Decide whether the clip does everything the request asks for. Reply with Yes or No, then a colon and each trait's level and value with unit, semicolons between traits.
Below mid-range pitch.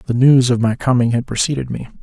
Yes: low, 125 Hz